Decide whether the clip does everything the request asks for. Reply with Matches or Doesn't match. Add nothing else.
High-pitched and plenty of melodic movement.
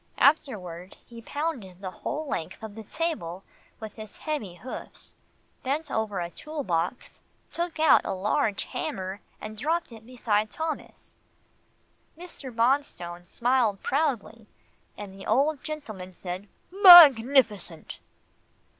Matches